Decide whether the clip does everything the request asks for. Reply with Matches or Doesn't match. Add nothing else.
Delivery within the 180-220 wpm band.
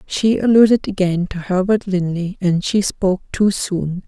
Doesn't match